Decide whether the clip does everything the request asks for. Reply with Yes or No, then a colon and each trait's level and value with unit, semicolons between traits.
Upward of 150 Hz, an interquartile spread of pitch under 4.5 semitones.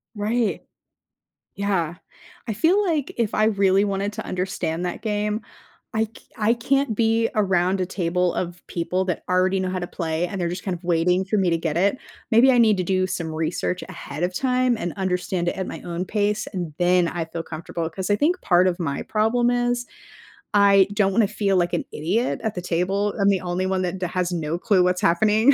Yes: high, 190 Hz; average, 3.3 semitones